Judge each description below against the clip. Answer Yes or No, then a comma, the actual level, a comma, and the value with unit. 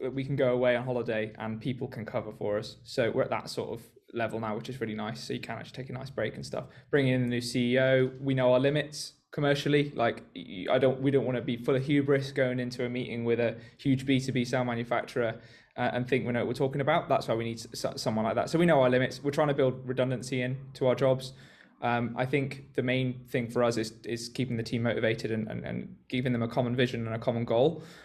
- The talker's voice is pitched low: Yes, low, 125 Hz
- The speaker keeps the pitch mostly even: Yes, narrow, 2.1 semitones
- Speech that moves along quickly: Yes, fast, 265 wpm